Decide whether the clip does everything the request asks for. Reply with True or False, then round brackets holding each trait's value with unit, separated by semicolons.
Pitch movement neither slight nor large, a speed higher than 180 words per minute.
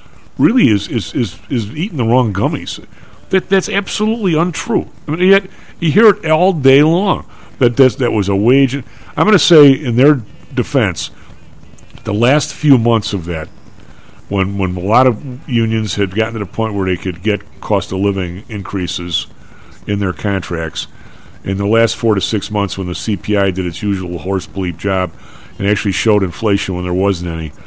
False (6.1 semitones; 190 wpm)